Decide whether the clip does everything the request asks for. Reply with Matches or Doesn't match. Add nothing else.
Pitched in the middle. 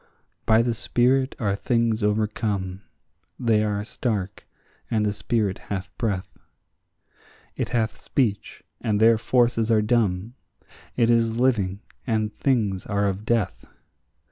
Doesn't match